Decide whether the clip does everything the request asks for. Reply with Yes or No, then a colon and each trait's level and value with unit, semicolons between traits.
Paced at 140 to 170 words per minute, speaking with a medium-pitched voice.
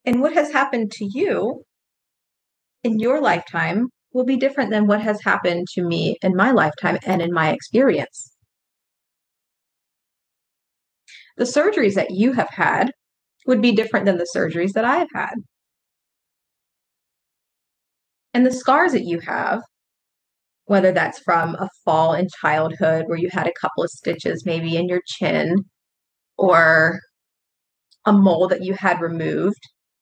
No: average, 145 wpm; high, 195 Hz